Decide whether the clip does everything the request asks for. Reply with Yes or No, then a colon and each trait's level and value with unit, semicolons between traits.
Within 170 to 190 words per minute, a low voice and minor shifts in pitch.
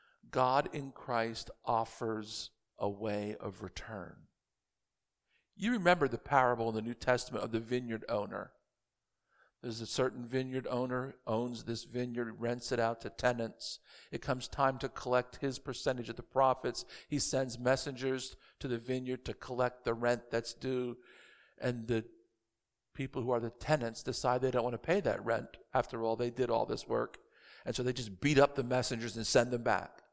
Yes: average, 175 wpm; low, 125 Hz; narrow, 2.2 semitones